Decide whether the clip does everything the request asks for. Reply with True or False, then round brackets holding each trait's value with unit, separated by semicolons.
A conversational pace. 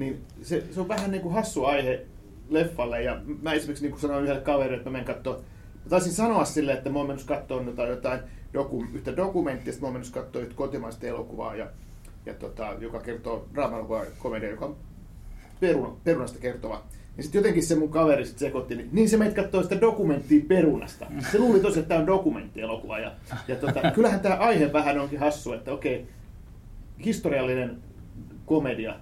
False (185 wpm)